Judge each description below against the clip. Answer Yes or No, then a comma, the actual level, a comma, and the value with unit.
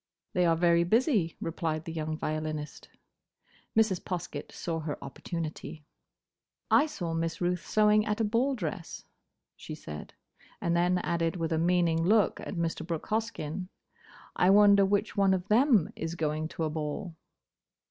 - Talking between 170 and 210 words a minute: No, average, 150 wpm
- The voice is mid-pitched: Yes, medium, 170 Hz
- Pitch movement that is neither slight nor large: Yes, average, 3.7 semitones